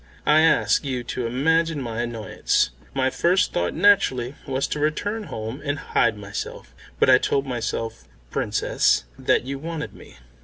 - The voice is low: Yes, low, 130 Hz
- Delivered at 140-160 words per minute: Yes, average, 155 wpm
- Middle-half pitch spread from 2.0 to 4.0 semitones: No, average, 4.9 semitones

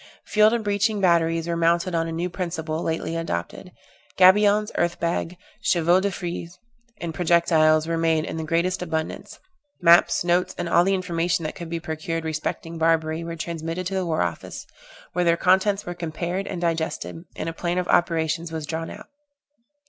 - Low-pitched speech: No, medium, 170 Hz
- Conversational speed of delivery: Yes, average, 180 wpm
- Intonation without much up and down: Yes, narrow, 1.6 semitones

